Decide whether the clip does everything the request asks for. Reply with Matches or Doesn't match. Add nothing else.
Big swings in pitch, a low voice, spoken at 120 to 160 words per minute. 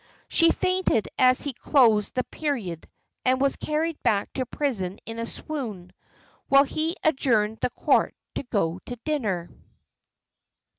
Doesn't match